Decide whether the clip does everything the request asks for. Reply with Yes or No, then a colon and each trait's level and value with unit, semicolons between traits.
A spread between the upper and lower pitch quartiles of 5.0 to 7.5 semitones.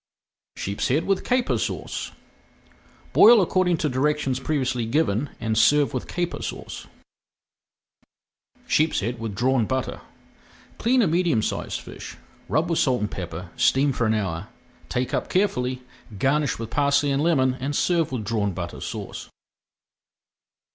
Yes: wide, 5.6 semitones